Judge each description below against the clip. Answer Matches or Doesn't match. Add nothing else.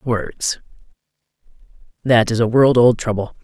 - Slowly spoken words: Matches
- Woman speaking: Doesn't match